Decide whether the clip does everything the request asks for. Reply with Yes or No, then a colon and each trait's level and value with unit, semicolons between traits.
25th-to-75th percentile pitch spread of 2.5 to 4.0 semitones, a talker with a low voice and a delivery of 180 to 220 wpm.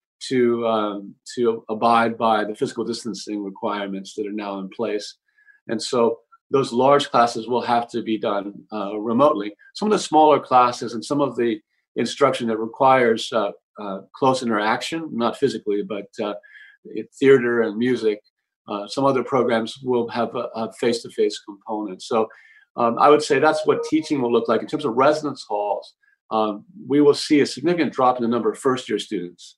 No: average, 4.8 semitones; low, 120 Hz; average, 185 wpm